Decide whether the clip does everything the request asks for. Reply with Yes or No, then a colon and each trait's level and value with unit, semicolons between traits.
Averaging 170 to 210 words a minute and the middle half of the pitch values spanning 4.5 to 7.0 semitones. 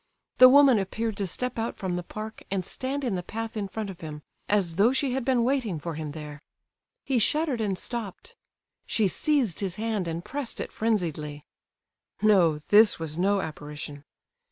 Yes: average, 180 wpm; wide, 5.6 semitones